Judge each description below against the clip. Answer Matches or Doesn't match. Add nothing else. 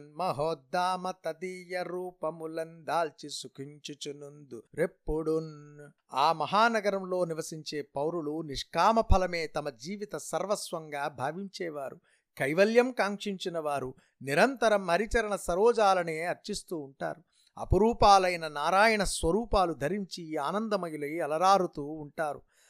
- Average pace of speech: Doesn't match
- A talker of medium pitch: Matches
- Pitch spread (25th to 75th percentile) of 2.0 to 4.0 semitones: Doesn't match